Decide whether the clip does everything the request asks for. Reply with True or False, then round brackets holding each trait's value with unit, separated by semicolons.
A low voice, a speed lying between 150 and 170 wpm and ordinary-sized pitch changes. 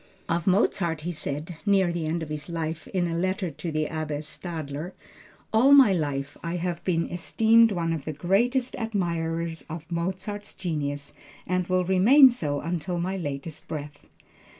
False (170 Hz; 165 wpm; 3.3 semitones)